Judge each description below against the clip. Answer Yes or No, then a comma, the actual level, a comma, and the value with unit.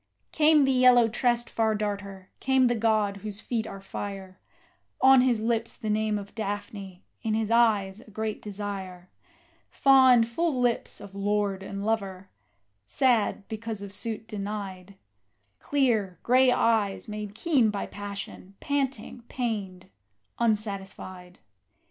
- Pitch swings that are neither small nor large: Yes, average, 3.1 semitones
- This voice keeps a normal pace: No, slow, 130 wpm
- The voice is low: No, high, 215 Hz